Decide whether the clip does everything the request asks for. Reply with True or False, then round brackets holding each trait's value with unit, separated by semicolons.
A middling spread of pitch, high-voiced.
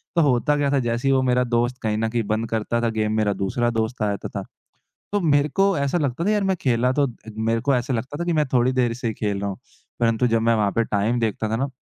False (3.6 semitones; 120 Hz)